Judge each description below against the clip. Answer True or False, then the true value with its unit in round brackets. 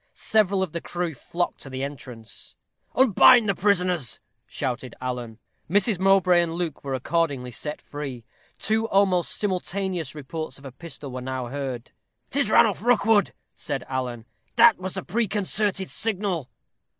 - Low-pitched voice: False (170 Hz)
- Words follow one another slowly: False (145 wpm)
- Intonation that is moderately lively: False (6.8 semitones)